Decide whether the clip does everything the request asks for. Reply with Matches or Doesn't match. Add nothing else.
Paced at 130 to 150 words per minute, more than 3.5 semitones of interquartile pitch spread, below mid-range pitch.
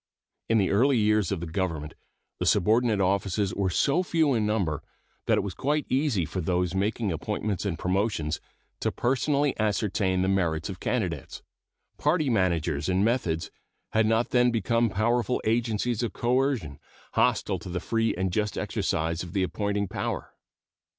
Doesn't match